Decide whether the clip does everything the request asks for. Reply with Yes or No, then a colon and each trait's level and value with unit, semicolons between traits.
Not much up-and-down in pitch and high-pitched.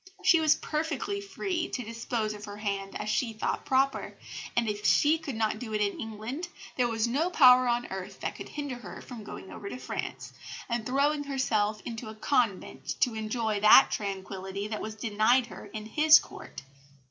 No: average, 4.1 semitones; high, 230 Hz